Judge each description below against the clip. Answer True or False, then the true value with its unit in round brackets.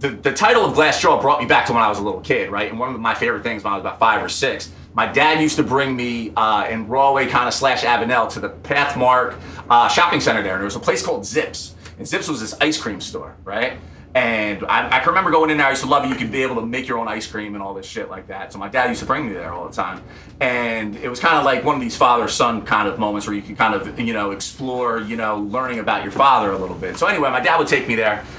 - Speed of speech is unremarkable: False (300 wpm)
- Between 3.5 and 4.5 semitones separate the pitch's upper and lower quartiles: True (3.9 semitones)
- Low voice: True (120 Hz)